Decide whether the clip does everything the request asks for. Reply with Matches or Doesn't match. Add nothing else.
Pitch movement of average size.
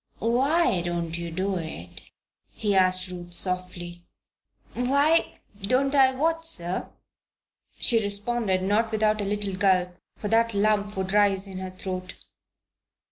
Matches